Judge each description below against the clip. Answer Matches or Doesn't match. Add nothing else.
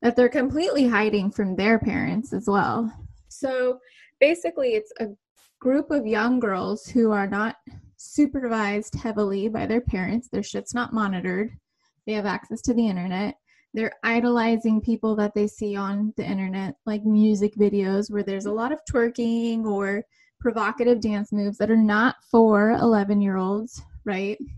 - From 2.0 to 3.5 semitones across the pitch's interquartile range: Matches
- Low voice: Doesn't match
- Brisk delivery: Doesn't match